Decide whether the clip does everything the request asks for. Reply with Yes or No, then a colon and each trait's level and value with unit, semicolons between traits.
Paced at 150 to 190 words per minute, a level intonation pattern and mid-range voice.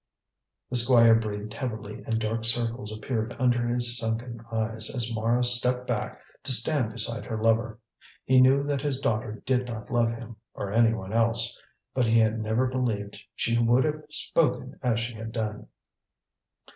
No: average, 165 wpm; narrow, 2.0 semitones; low, 115 Hz